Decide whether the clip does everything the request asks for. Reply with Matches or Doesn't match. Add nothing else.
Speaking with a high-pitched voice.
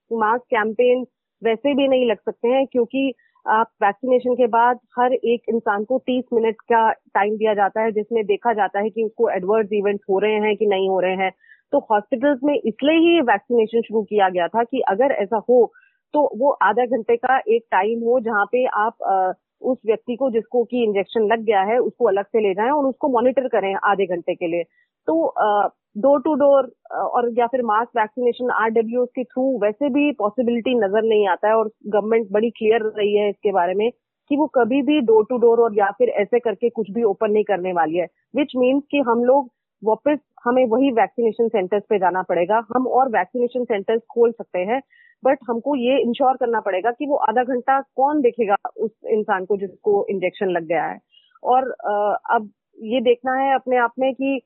Matches